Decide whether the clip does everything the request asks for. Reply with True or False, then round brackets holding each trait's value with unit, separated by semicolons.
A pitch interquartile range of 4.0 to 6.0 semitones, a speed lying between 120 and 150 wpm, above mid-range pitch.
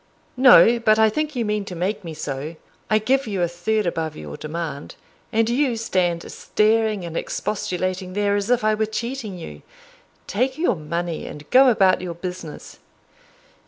False (4.5 semitones; 170 wpm; 200 Hz)